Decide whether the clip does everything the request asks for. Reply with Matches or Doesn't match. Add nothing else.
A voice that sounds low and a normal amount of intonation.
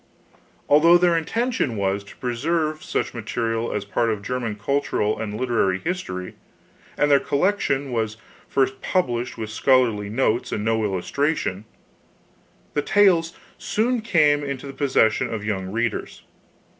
Doesn't match